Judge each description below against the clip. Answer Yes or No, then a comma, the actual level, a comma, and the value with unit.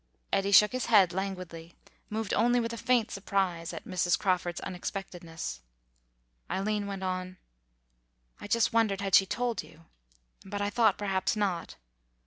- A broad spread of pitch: No, average, 2.7 semitones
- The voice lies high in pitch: Yes, high, 195 Hz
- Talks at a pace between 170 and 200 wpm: No, average, 145 wpm